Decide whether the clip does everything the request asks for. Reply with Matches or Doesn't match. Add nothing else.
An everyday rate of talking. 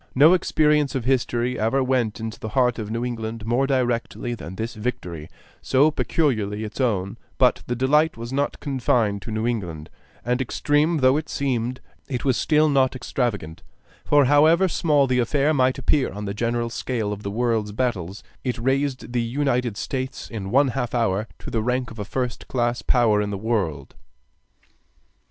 Matches